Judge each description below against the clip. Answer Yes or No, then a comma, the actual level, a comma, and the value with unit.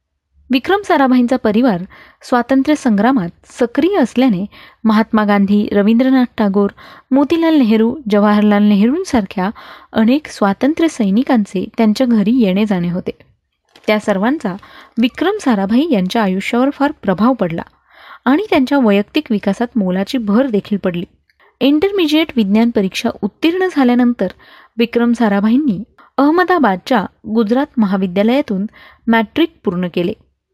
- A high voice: Yes, high, 230 Hz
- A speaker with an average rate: Yes, average, 100 wpm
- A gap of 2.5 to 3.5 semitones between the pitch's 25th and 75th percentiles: No, average, 4.5 semitones